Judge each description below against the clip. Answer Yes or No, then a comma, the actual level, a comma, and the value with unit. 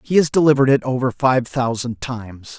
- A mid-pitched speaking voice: No, low, 130 Hz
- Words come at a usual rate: Yes, average, 185 wpm